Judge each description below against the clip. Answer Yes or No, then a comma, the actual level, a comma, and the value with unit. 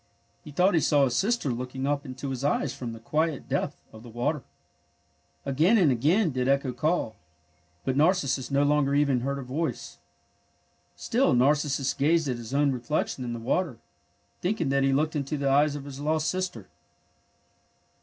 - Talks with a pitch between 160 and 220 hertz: No, medium, 140 Hz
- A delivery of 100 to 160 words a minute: No, average, 175 wpm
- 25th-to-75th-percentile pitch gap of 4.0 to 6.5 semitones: No, average, 3.0 semitones